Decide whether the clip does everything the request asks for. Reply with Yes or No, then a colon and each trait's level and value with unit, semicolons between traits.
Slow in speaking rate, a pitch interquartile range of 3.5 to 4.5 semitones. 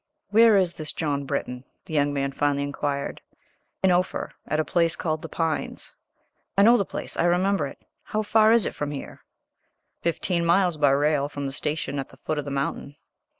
No: average, 195 wpm; average, 4.1 semitones